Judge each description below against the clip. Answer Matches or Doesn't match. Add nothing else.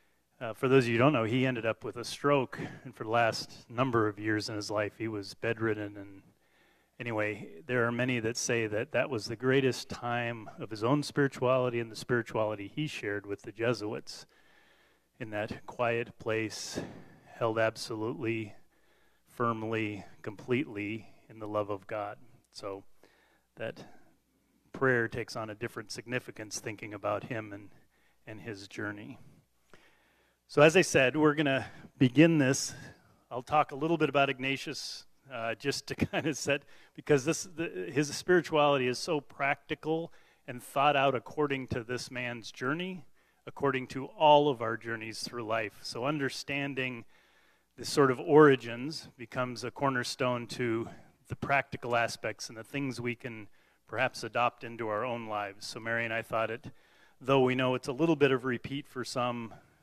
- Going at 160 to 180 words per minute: Matches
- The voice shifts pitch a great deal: Doesn't match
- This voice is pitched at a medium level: Doesn't match